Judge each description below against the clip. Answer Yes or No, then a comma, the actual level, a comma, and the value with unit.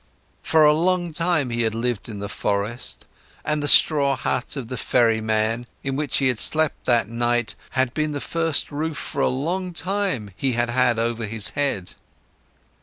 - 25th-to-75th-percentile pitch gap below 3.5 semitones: No, average, 4.8 semitones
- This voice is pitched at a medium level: No, low, 130 Hz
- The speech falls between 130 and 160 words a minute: No, average, 180 wpm